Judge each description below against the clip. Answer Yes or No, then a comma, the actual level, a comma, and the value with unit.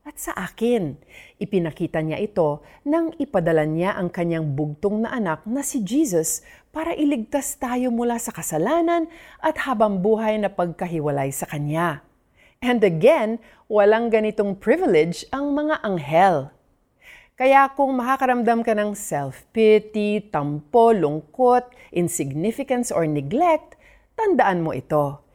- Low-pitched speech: No, high, 215 Hz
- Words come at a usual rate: Yes, average, 125 wpm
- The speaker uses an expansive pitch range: Yes, wide, 7.8 semitones